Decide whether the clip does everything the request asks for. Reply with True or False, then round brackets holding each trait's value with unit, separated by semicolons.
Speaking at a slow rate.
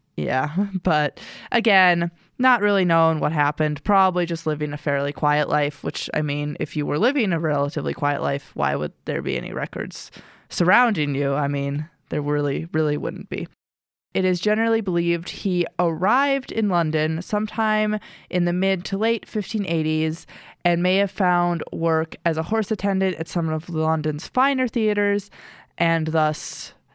False (165 wpm)